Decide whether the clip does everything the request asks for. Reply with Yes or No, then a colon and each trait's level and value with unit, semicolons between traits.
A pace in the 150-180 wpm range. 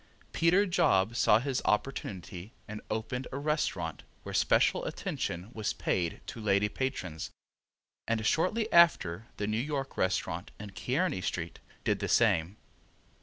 No: slow, 135 wpm